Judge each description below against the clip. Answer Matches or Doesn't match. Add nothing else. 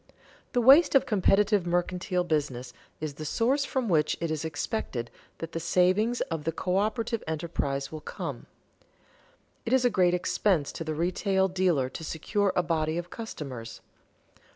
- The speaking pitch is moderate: Matches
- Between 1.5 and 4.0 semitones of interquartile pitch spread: Doesn't match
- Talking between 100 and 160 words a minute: Matches